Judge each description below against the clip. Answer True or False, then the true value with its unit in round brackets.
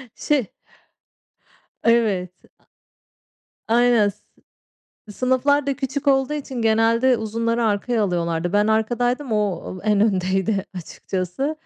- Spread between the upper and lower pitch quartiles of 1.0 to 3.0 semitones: False (4.0 semitones)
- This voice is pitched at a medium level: False (225 Hz)